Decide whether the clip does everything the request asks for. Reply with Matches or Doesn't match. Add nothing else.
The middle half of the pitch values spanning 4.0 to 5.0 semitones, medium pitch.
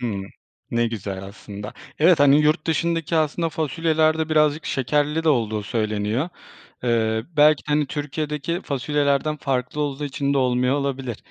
Matches